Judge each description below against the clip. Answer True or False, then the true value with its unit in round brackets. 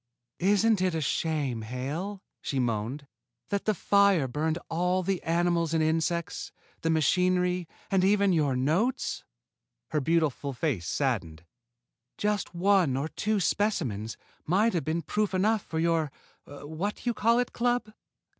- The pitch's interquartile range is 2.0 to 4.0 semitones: False (5.4 semitones)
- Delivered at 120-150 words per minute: True (140 wpm)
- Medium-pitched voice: True (170 Hz)